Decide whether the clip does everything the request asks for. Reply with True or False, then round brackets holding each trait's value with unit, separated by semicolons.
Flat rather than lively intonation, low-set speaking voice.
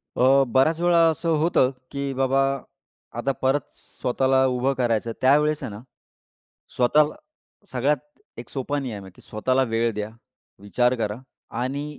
False (3.1 semitones; 130 Hz)